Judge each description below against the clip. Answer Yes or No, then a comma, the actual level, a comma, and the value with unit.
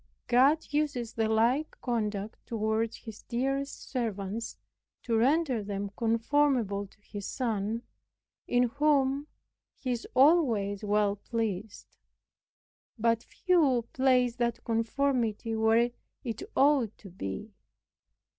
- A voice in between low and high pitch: No, high, 230 Hz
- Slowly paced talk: Yes, slow, 110 wpm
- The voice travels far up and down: No, average, 3.4 semitones